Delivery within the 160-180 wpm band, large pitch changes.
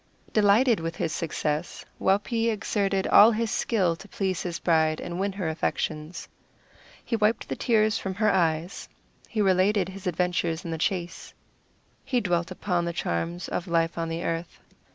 No: average, 165 wpm; average, 3.7 semitones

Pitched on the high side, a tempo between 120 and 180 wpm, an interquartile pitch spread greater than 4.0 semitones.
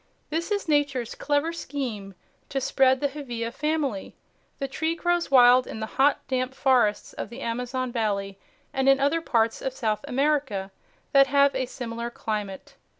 No: very high, 260 Hz; average, 160 wpm; average, 3.7 semitones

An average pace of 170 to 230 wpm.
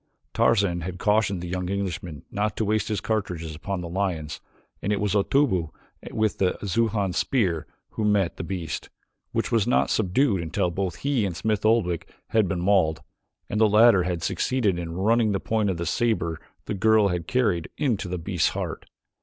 Yes: average, 185 wpm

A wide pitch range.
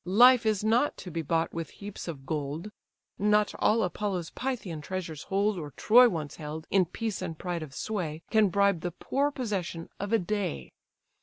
No: average, 4.5 semitones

